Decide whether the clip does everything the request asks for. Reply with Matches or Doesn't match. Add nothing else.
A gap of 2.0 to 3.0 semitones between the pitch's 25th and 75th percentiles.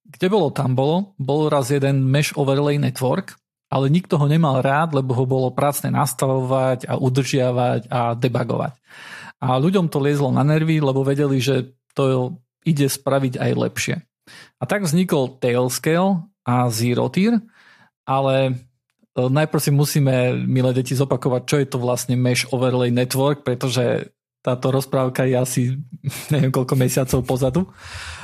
Matches